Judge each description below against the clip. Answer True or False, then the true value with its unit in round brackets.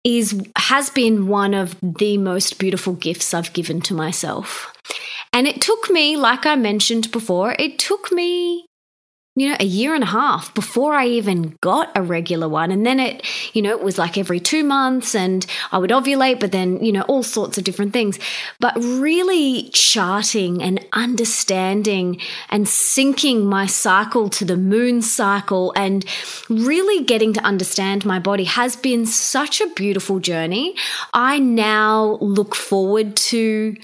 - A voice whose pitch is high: True (215 Hz)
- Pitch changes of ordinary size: True (4.7 semitones)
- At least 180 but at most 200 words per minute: False (165 wpm)